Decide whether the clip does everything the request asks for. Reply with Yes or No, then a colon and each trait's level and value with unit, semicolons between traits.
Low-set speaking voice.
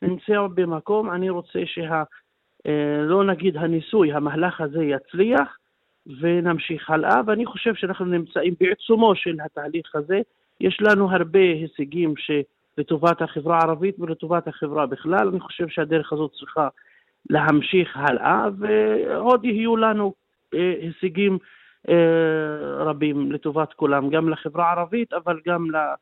No: medium, 170 Hz